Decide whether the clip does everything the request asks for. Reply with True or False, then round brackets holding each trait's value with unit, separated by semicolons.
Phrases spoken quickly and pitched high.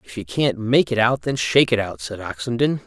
False (250 wpm; 120 Hz)